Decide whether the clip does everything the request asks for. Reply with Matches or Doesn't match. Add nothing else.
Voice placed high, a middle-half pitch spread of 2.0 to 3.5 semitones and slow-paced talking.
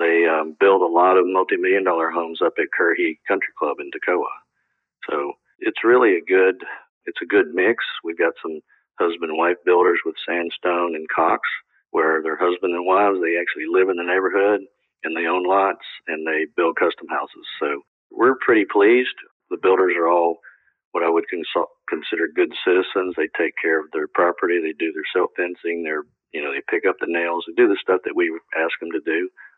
Doesn't match